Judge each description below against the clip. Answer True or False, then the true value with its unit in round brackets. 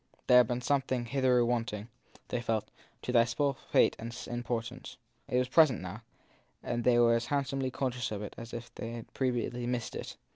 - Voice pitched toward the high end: False (120 Hz)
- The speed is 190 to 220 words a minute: True (195 wpm)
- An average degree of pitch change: False (1.5 semitones)